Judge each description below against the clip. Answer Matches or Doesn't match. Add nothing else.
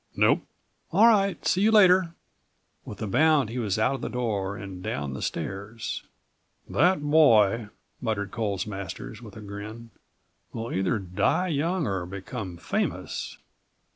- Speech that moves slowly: Doesn't match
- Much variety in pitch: Matches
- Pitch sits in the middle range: Doesn't match